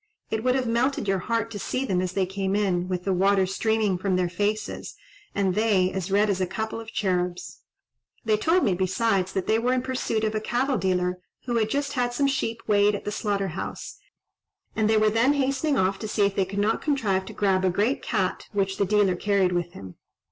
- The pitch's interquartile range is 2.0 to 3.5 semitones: Yes, average, 3.2 semitones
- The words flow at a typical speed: No, fast, 225 wpm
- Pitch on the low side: No, high, 205 Hz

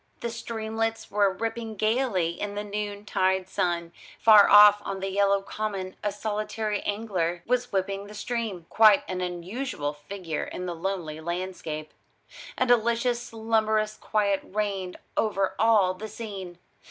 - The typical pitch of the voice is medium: No, high, 205 Hz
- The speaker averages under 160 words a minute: Yes, average, 140 wpm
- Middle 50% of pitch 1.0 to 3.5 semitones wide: Yes, average, 2.8 semitones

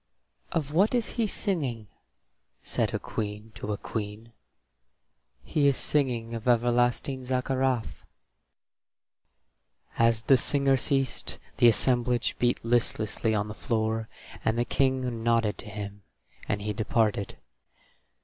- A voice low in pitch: Yes, low, 120 Hz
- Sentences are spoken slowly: Yes, slow, 120 wpm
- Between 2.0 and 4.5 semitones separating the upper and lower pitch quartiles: Yes, average, 3.1 semitones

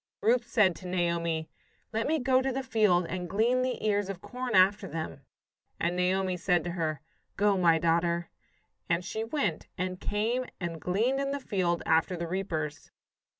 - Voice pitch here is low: No, medium, 185 Hz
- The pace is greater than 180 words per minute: No, average, 175 wpm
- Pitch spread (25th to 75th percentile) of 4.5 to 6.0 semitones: Yes, average, 4.8 semitones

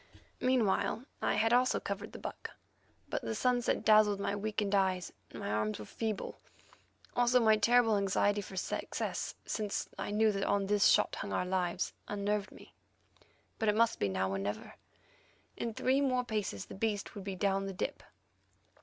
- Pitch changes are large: No, narrow, 2.5 semitones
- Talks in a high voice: Yes, high, 205 Hz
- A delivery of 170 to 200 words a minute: Yes, average, 175 wpm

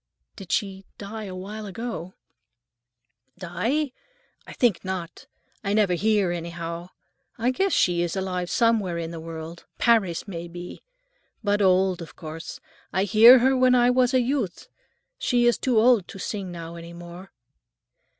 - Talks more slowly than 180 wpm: Yes, average, 160 wpm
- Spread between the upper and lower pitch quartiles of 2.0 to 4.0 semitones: No, average, 4.9 semitones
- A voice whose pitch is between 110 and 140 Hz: No, high, 190 Hz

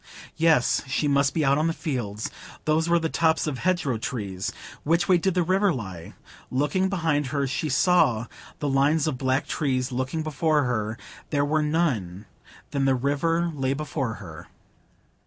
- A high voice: No, medium, 145 Hz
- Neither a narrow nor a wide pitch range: Yes, average, 4.1 semitones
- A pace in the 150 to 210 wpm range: Yes, average, 170 wpm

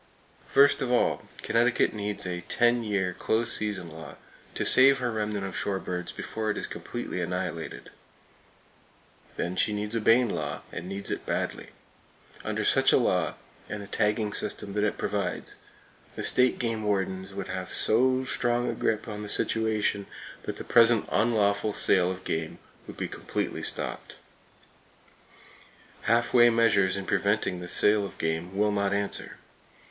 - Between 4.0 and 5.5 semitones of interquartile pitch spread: No, average, 3.3 semitones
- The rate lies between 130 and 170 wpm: Yes, average, 160 wpm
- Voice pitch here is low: Yes, low, 105 Hz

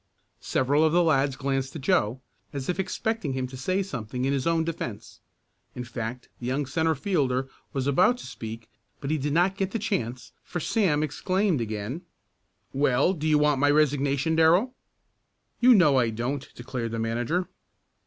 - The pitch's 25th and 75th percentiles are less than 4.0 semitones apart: No, average, 4.8 semitones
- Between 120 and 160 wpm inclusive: No, average, 175 wpm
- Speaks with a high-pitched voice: No, medium, 140 Hz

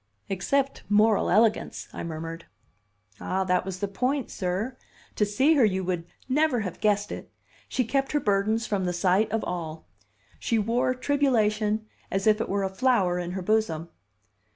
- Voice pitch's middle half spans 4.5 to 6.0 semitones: No, average, 4.1 semitones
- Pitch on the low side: No, high, 210 Hz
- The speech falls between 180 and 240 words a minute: No, average, 170 wpm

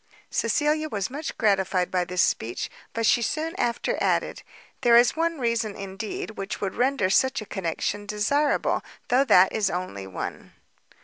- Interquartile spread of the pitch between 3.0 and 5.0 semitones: No, wide, 5.6 semitones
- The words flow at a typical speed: Yes, average, 160 wpm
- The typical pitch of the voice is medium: No, high, 215 Hz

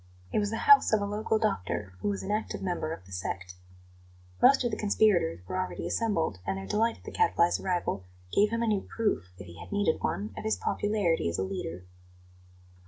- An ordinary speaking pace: No, fast, 215 wpm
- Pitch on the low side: No, medium, 185 Hz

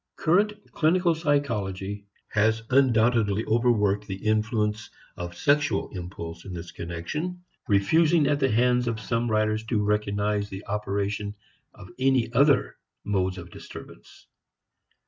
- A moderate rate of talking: No, slow, 125 wpm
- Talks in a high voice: No, low, 110 Hz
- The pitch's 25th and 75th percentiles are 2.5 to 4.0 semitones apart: No, average, 4.5 semitones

